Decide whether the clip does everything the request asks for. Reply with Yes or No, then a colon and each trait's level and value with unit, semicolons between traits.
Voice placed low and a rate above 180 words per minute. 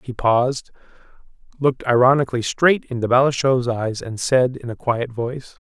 No: low, 125 Hz; average, 150 wpm